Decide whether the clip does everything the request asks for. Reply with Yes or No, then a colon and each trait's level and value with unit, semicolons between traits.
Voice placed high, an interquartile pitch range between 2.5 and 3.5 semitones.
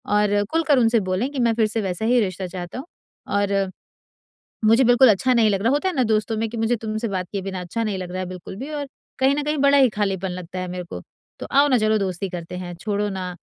No: high, 215 Hz; average, 4.5 semitones